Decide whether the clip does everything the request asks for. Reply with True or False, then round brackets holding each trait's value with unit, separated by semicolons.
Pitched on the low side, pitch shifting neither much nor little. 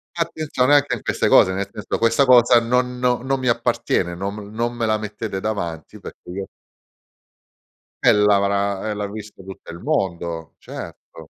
True (105 Hz; 3.9 semitones)